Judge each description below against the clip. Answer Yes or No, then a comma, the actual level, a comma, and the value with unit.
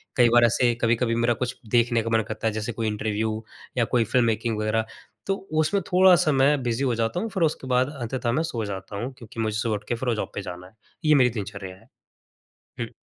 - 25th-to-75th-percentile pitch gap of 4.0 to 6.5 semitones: No, average, 2.7 semitones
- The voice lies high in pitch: No, low, 115 Hz